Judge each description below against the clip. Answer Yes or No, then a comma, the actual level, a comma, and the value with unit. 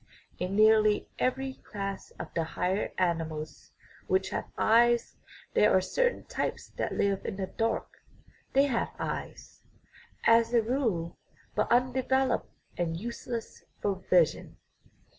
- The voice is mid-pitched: No, high, 215 Hz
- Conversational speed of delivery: No, slow, 125 wpm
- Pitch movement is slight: No, average, 4.7 semitones